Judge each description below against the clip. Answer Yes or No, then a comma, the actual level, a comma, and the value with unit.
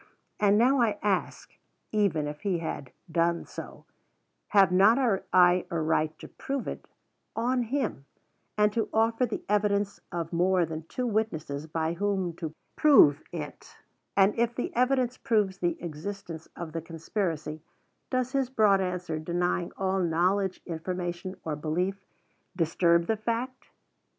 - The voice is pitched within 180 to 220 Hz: Yes, medium, 185 Hz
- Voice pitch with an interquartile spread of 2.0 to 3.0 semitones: No, average, 4.6 semitones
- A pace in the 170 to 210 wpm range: No, average, 145 wpm